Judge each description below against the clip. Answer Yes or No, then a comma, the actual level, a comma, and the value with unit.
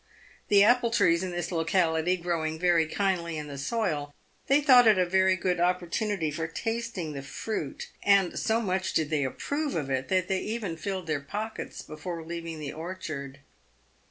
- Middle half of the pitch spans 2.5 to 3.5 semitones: No, average, 4.0 semitones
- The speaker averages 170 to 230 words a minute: Yes, average, 175 wpm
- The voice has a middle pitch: Yes, medium, 175 Hz